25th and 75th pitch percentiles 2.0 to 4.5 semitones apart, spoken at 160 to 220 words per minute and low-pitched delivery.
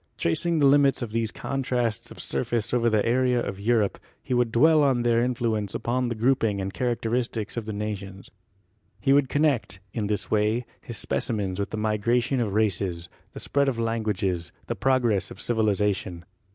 Yes: average, 3.2 semitones; average, 180 wpm; low, 115 Hz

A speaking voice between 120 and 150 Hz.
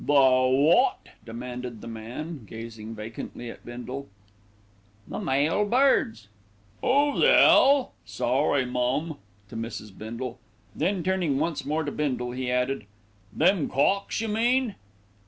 Yes: low, 135 Hz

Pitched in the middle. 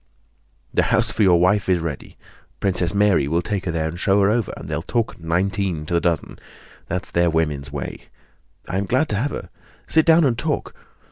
No: very low, 95 Hz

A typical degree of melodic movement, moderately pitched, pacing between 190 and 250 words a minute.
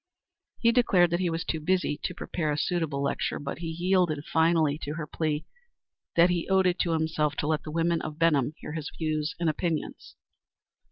No: narrow, 2.3 semitones; medium, 160 Hz; average, 200 wpm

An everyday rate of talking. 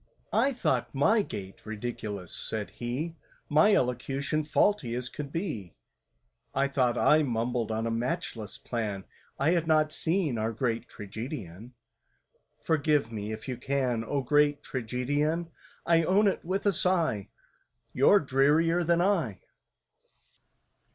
No: slow, 130 wpm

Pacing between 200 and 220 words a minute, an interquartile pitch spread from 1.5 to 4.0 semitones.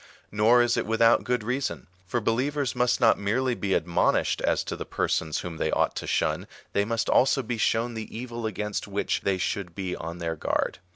Yes: fast, 205 wpm; average, 3.7 semitones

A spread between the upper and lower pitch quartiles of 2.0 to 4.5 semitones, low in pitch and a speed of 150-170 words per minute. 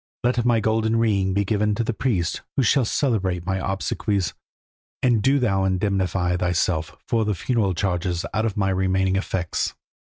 Yes: average, 3.2 semitones; low, 100 Hz; average, 165 wpm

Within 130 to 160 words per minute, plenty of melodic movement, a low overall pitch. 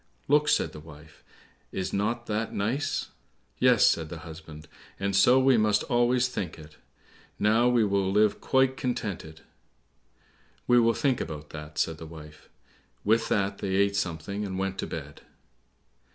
Yes: average, 150 wpm; wide, 6.7 semitones; low, 100 Hz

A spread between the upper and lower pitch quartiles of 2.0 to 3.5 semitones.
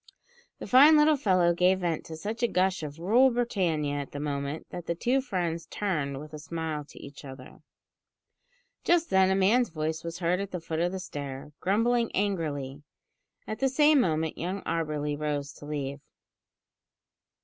No: average, 5.3 semitones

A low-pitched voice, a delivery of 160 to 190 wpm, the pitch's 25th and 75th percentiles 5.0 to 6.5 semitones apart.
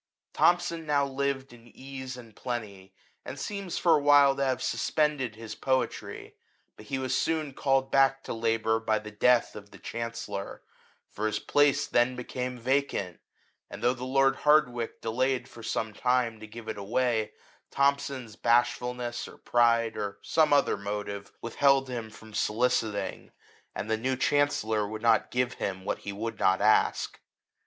No: low, 120 Hz; average, 165 wpm; average, 3.6 semitones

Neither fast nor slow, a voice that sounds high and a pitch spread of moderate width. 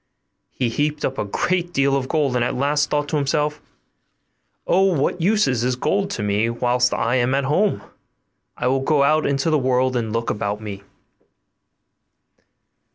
No: average, 175 wpm; low, 135 Hz; average, 3.7 semitones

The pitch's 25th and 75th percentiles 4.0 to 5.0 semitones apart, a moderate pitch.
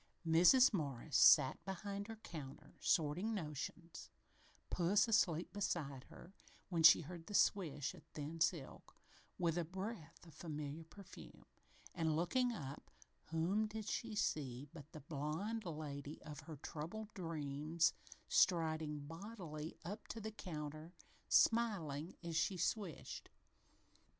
Yes: average, 4.7 semitones; medium, 165 Hz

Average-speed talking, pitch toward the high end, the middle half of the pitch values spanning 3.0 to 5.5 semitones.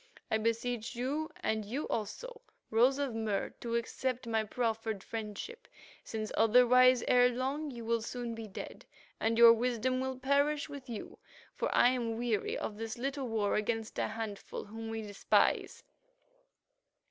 No: average, 155 wpm; high, 235 Hz; narrow, 2.5 semitones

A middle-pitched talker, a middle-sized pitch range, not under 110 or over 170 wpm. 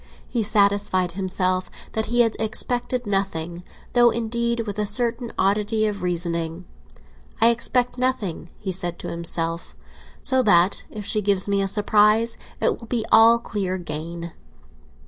No: high, 205 Hz; average, 4.1 semitones; average, 145 wpm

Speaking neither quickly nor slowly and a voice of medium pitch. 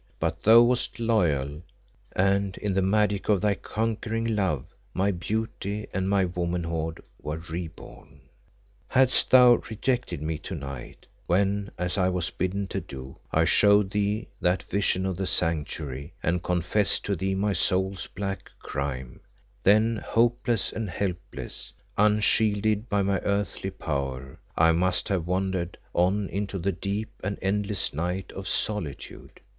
No: average, 145 wpm; very low, 95 Hz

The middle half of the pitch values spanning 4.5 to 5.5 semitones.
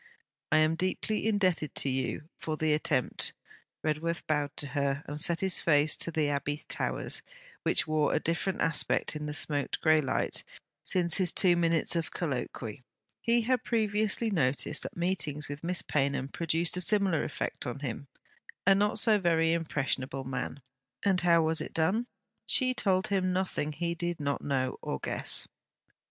No: average, 4.1 semitones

